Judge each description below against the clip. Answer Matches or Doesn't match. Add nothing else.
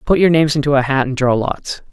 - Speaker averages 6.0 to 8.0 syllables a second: Matches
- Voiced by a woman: Doesn't match